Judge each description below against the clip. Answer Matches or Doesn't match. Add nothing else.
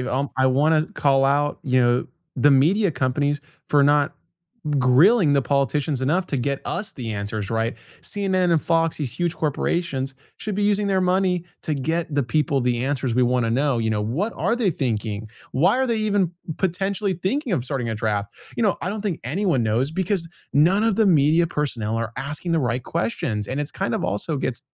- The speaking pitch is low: Doesn't match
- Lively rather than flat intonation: Matches